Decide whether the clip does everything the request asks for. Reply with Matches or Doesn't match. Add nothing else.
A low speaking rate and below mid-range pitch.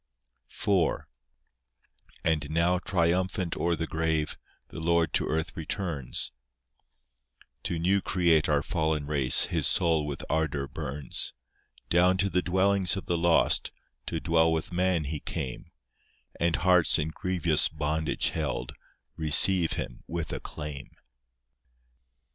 Matches